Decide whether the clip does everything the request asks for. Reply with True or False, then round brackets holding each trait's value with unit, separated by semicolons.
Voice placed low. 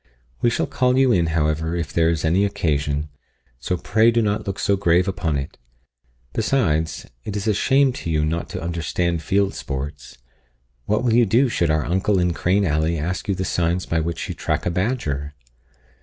True (85 Hz)